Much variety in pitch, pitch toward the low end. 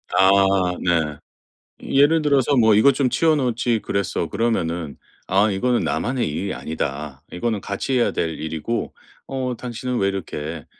Yes: wide, 7.1 semitones; low, 110 Hz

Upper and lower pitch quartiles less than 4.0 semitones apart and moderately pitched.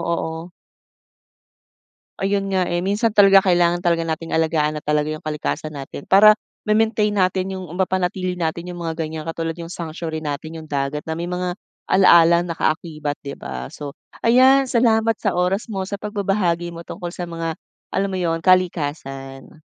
Yes: average, 3.3 semitones; medium, 175 Hz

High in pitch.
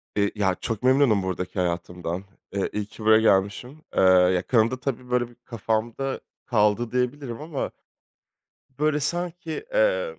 No: low, 115 Hz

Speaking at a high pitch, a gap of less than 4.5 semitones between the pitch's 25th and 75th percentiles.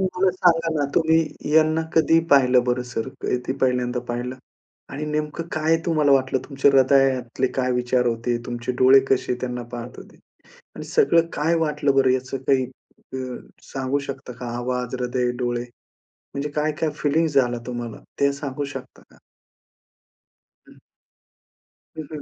No: low, 135 Hz; average, 3.3 semitones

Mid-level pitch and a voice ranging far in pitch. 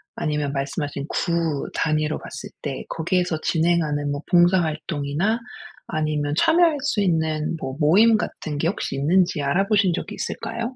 No: medium, 160 Hz; average, 3.9 semitones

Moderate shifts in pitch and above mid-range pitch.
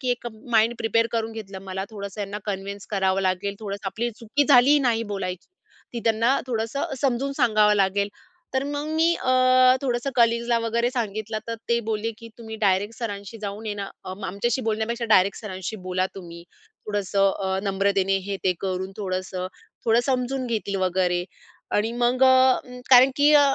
Yes: average, 3.5 semitones; high, 220 Hz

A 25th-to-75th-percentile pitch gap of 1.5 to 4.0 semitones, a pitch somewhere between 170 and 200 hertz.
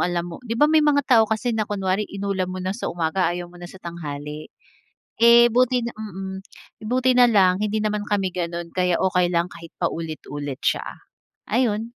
No: average, 4.4 semitones; high, 190 Hz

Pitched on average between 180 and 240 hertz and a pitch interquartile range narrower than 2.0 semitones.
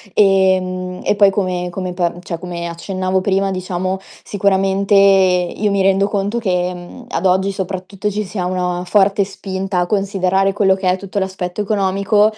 Yes: high, 190 Hz; narrow, 1.4 semitones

